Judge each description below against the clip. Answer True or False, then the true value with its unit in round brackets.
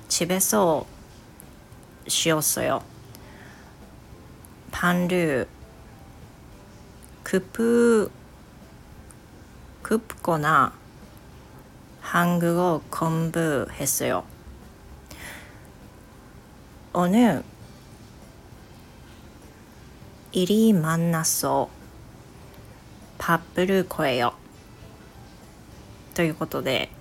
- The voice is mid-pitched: True (160 Hz)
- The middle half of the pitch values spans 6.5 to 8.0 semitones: False (8.9 semitones)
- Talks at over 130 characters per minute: False (125 characters per minute)